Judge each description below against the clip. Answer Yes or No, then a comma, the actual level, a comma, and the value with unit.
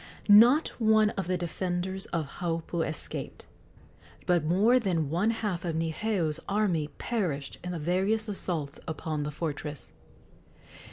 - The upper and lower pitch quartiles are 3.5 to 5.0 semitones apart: Yes, average, 4.3 semitones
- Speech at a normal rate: No, slow, 130 wpm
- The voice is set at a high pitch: No, medium, 175 Hz